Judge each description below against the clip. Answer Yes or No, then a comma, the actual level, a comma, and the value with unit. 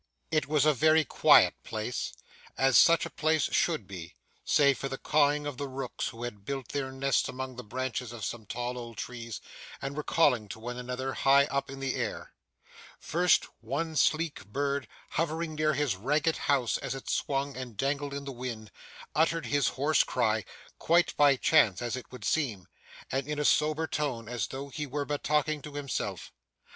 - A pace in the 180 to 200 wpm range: Yes, average, 190 wpm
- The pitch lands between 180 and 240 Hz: No, low, 135 Hz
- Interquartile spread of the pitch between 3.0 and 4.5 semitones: Yes, average, 3.3 semitones